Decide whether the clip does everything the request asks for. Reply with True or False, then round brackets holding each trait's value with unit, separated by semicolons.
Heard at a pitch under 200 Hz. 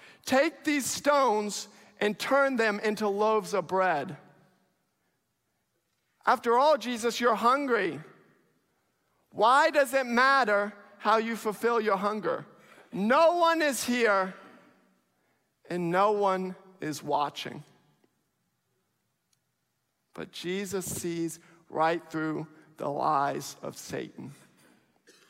False (205 Hz)